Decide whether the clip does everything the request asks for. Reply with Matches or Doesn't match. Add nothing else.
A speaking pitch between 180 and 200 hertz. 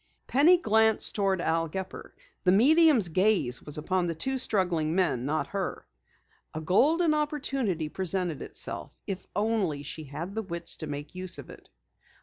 Matches